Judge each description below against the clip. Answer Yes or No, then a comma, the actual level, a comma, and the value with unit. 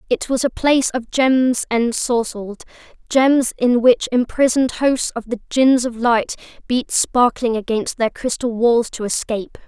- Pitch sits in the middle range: No, high, 245 Hz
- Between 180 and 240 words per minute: No, average, 155 wpm